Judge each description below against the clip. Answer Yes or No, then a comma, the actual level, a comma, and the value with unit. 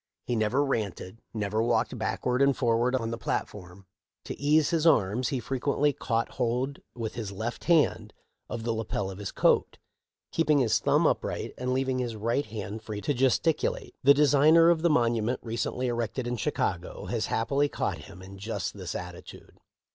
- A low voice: Yes, low, 120 Hz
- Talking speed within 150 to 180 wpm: Yes, average, 175 wpm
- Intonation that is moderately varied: Yes, average, 4.1 semitones